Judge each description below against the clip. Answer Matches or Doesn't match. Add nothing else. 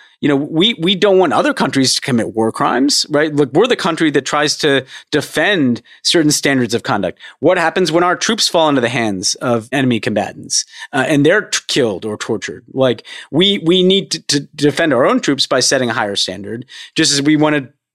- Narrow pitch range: Doesn't match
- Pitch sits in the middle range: Matches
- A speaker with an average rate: Doesn't match